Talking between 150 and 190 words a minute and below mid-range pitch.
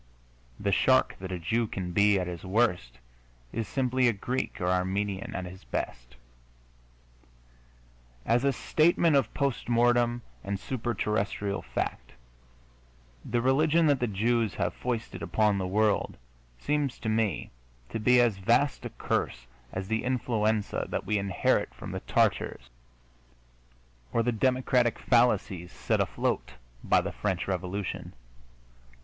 No: average, 140 wpm; low, 110 Hz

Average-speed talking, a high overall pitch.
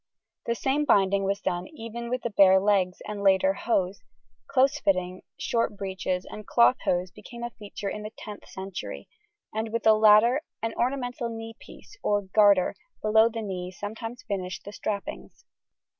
Yes: average, 165 wpm; high, 210 Hz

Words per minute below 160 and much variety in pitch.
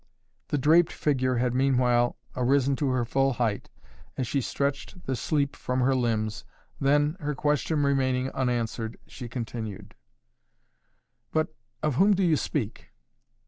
No: average, 140 wpm; average, 3.1 semitones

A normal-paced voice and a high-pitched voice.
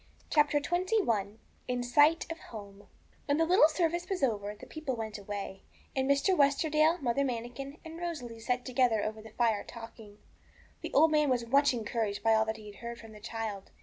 Yes: average, 185 wpm; high, 245 Hz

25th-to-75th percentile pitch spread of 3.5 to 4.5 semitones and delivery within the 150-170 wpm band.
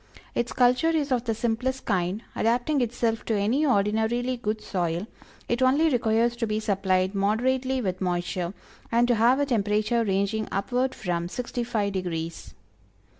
Yes: average, 3.8 semitones; average, 155 wpm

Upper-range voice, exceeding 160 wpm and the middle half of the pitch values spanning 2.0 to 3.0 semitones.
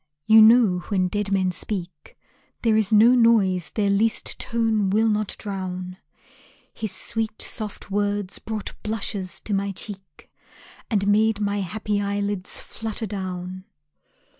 No: high, 205 Hz; slow, 135 wpm; narrow, 2.4 semitones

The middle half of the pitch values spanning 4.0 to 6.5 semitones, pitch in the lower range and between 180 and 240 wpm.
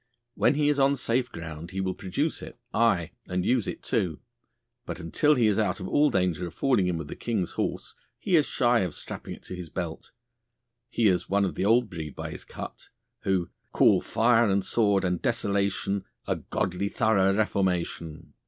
Yes: average, 4.6 semitones; low, 100 Hz; average, 195 wpm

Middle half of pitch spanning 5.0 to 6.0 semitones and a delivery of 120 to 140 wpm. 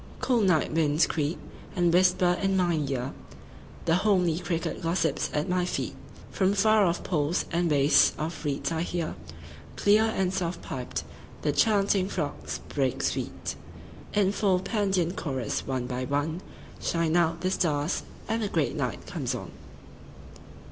No: average, 4.4 semitones; slow, 135 wpm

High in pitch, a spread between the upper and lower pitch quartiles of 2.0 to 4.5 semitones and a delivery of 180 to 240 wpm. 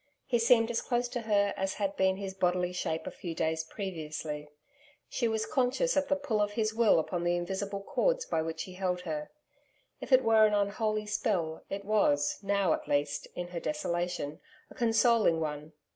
No: high, 195 Hz; average, 5.2 semitones; average, 190 wpm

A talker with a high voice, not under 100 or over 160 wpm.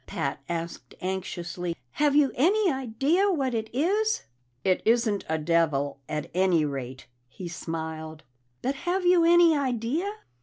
Yes: high, 220 Hz; average, 140 wpm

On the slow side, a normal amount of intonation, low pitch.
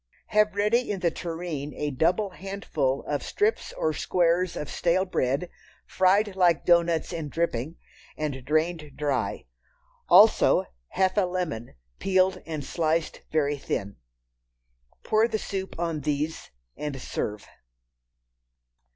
No: slow, 125 wpm; average, 4.1 semitones; medium, 170 Hz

